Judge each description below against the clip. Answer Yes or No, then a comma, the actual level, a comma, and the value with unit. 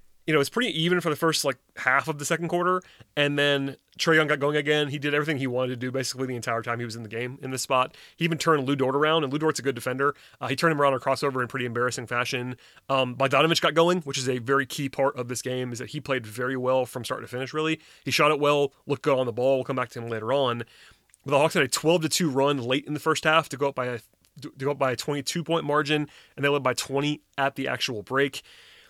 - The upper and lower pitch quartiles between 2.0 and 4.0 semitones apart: Yes, average, 2.8 semitones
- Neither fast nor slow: No, fast, 290 wpm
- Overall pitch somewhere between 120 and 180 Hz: Yes, medium, 140 Hz